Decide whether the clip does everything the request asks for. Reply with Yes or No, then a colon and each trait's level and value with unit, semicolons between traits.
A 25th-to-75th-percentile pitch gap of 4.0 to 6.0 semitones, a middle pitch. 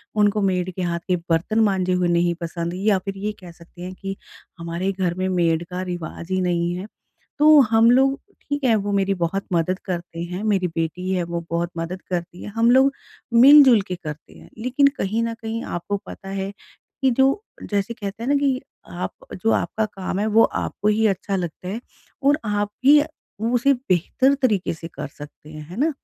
No: average, 4.4 semitones; high, 195 Hz